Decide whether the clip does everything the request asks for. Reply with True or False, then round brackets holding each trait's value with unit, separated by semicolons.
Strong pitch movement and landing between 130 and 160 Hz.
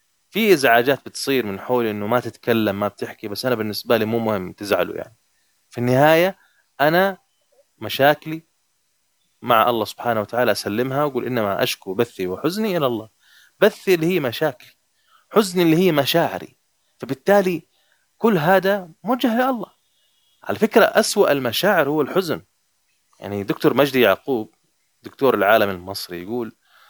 True (8.2 semitones; 135 Hz)